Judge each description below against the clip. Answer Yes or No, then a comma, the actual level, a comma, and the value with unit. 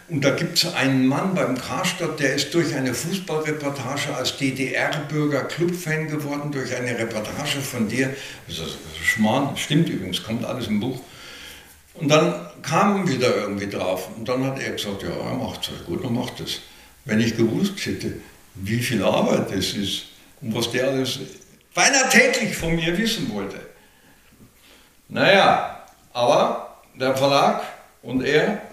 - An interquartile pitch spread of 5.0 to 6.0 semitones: Yes, wide, 5.6 semitones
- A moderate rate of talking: Yes, average, 160 wpm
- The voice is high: No, low, 135 Hz